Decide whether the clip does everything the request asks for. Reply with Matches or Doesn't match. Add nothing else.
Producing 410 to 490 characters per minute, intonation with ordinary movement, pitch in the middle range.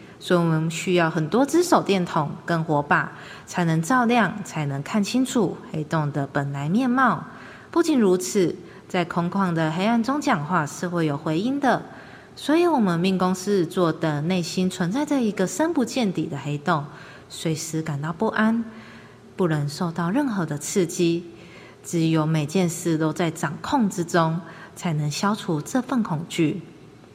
Doesn't match